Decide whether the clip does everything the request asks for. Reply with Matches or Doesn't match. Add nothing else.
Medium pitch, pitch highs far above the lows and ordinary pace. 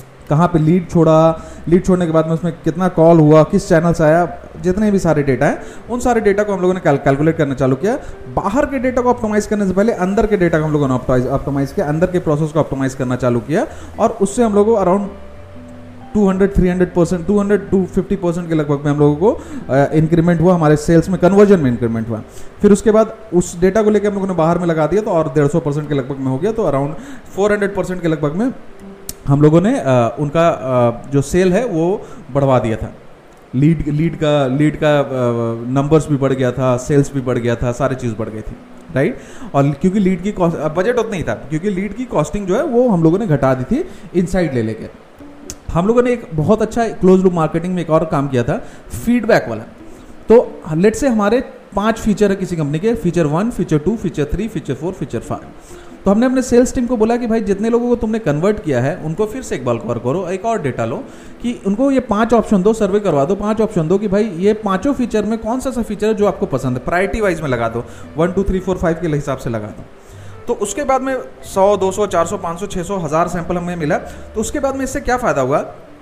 Doesn't match